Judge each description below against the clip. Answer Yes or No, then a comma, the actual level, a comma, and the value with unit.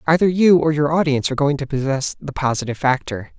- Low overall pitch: No, medium, 145 Hz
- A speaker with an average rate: No, fast, 215 wpm